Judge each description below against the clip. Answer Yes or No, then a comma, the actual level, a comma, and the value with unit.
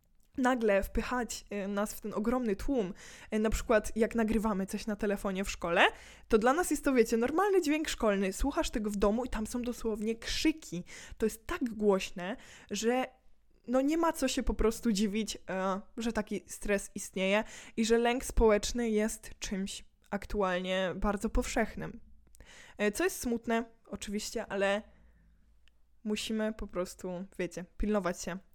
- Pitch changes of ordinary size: Yes, average, 3.1 semitones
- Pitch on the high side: Yes, high, 215 Hz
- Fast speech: No, average, 150 wpm